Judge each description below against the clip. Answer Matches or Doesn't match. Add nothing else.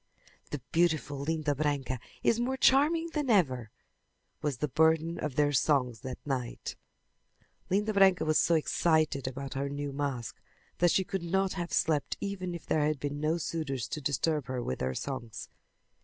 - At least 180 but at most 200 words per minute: Doesn't match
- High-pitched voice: Doesn't match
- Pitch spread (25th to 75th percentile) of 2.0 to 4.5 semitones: Matches